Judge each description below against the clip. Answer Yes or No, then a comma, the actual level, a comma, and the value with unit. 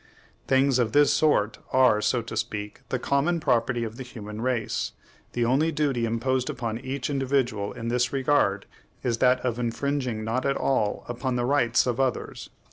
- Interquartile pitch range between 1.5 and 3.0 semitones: Yes, narrow, 2.6 semitones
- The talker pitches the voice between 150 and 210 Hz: No, low, 125 Hz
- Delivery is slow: No, average, 175 wpm